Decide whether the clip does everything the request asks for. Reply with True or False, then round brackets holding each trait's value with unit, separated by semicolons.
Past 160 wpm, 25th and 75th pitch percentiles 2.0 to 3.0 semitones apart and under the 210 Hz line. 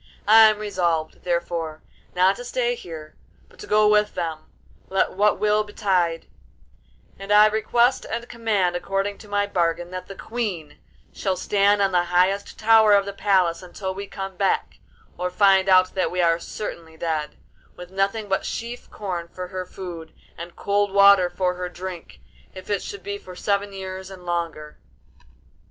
True (170 wpm; 2.6 semitones; 190 Hz)